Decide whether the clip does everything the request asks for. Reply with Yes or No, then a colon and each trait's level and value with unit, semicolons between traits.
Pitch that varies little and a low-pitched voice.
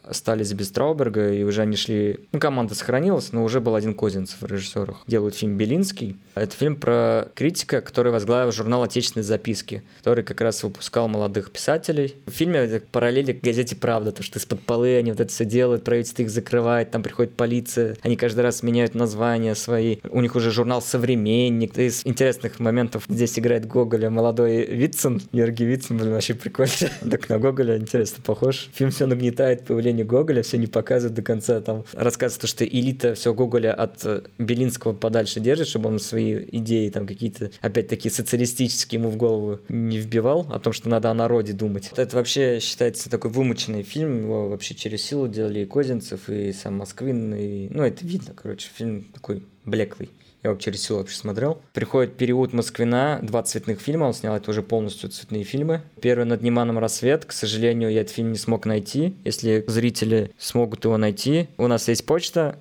Yes: narrow, 2.1 semitones; low, 115 Hz